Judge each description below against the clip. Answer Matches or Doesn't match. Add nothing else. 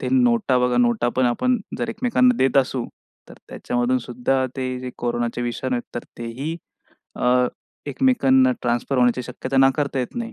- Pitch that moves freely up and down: Matches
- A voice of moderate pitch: Doesn't match